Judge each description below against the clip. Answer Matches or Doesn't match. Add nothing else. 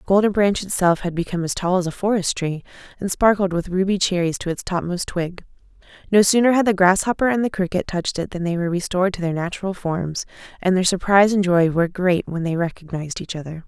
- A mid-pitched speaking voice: Matches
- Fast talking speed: Matches